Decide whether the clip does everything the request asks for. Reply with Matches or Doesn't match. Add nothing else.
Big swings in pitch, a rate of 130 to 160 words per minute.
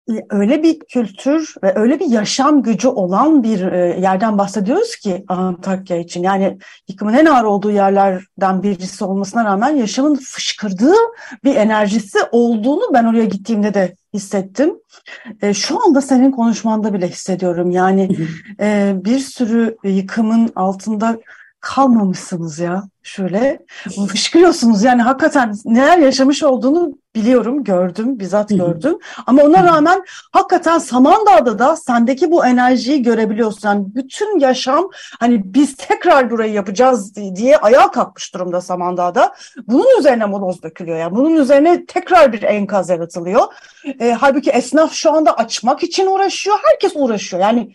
Matches